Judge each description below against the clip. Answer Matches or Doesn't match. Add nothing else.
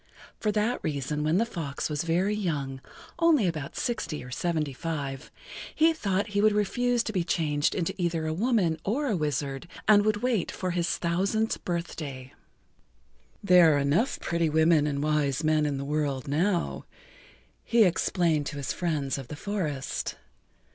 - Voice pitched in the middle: Matches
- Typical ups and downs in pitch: Doesn't match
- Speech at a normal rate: Matches